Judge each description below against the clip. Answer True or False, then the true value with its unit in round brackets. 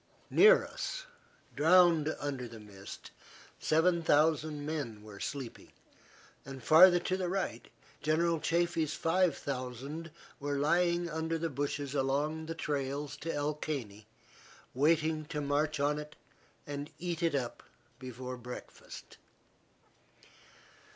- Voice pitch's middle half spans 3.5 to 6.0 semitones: False (3.1 semitones)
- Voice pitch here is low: False (150 Hz)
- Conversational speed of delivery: False (120 wpm)